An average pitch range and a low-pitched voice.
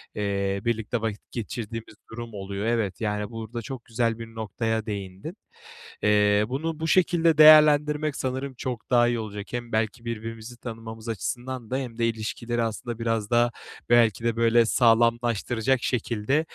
No: narrow, 2.0 semitones; low, 115 Hz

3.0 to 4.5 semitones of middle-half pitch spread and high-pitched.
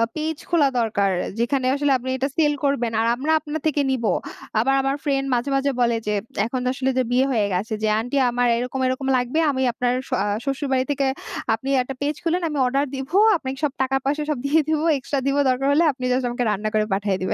No: narrow, 2.6 semitones; very high, 265 Hz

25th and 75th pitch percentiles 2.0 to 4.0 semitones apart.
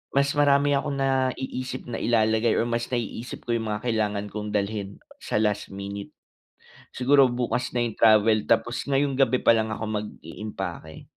Yes: average, 3.6 semitones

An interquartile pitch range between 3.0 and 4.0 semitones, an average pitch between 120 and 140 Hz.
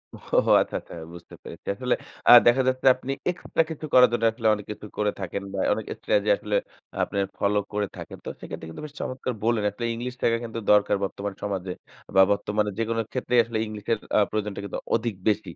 No: average, 3.3 semitones; low, 110 Hz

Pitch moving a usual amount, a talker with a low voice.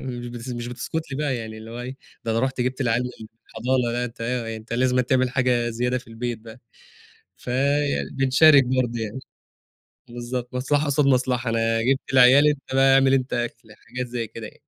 No: narrow, 1.9 semitones; low, 125 Hz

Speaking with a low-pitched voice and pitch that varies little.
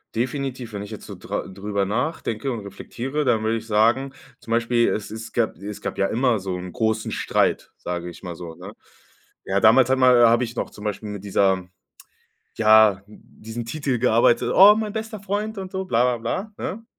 No: low, 115 Hz; average, 4.2 semitones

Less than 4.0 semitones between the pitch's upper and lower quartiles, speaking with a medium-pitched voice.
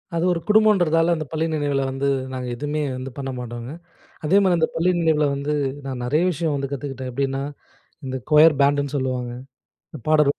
Yes: average, 3.2 semitones; medium, 145 Hz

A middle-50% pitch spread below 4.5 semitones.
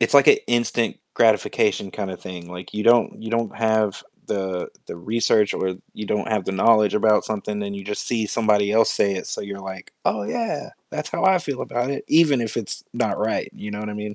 Yes: average, 2.7 semitones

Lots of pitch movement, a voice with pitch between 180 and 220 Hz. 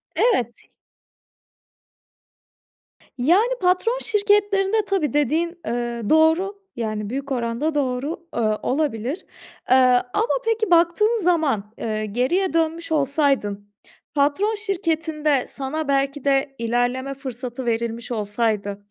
No: wide, 6.4 semitones; very high, 285 Hz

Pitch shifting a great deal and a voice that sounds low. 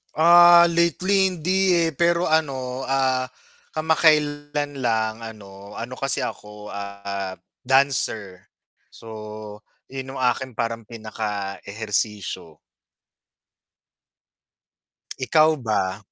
Yes: wide, 6.8 semitones; low, 130 Hz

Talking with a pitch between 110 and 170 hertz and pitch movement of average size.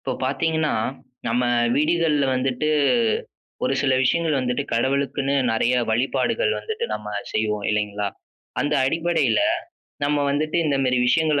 Yes: medium, 140 Hz; average, 3.8 semitones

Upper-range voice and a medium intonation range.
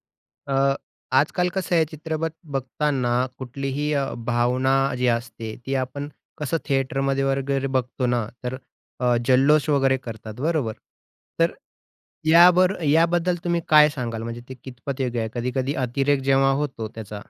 No: low, 135 Hz; average, 3.2 semitones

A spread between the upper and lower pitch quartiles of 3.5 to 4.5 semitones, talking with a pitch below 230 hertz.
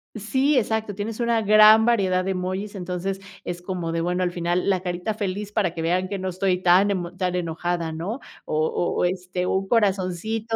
No: average, 2.9 semitones; medium, 185 Hz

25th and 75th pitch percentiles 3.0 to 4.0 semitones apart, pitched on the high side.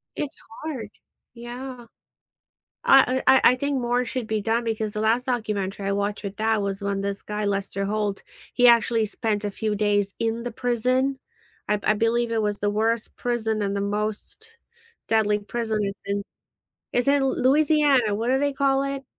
Yes: average, 3.3 semitones; high, 225 Hz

